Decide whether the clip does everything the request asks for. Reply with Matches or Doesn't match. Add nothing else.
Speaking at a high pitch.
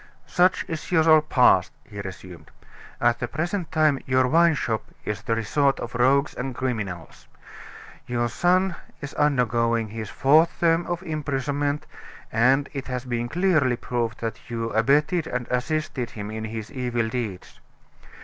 Doesn't match